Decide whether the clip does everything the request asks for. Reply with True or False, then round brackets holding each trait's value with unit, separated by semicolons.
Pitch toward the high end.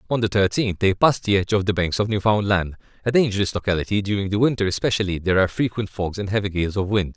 False (100 Hz)